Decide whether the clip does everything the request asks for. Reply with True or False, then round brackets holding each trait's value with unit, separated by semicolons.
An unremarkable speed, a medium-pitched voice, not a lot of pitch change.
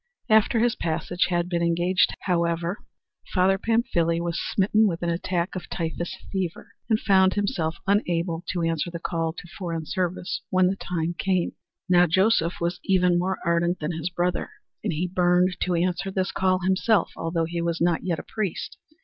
True (175 wpm; 175 Hz; 1.9 semitones)